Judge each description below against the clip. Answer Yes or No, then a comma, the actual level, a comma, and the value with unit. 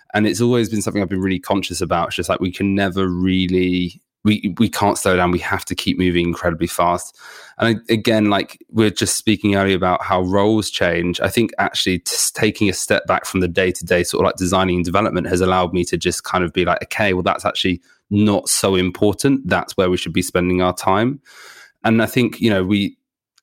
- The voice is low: Yes, very low, 95 Hz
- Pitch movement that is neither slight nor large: Yes, average, 3.0 semitones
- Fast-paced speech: Yes, fast, 230 wpm